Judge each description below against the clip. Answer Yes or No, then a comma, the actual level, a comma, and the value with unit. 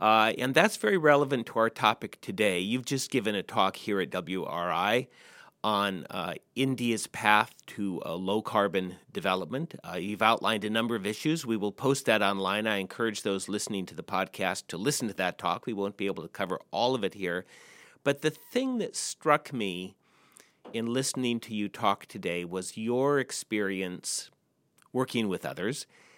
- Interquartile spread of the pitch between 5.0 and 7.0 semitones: No, average, 4.6 semitones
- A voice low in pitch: Yes, low, 110 Hz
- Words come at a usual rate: Yes, average, 180 wpm